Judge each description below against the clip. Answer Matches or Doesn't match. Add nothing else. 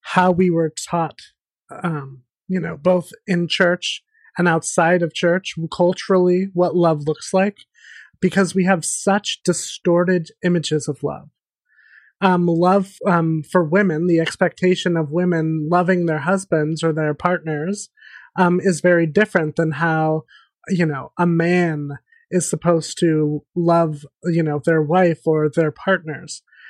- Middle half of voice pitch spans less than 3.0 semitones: Matches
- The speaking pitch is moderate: Matches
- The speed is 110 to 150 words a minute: Matches